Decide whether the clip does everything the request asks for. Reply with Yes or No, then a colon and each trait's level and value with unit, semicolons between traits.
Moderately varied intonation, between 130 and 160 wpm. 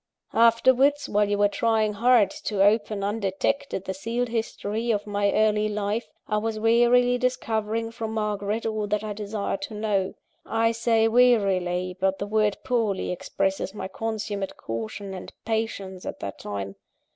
No: narrow, 2.2 semitones; average, 155 wpm